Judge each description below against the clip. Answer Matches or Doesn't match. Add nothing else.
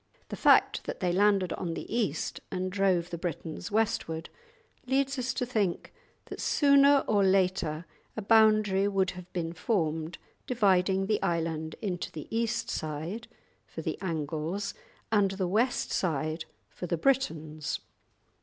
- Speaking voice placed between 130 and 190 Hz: Matches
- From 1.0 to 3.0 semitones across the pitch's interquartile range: Doesn't match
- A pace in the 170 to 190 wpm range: Doesn't match